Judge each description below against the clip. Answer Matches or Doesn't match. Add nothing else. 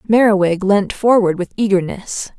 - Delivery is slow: Matches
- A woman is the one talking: Matches